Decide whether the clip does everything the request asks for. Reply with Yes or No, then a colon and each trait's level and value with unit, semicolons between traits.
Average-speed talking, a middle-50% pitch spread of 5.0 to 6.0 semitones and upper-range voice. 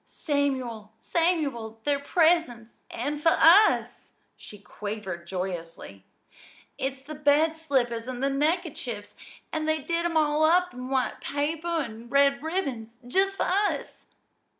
No: slow, 130 wpm; wide, 5.5 semitones; very high, 280 Hz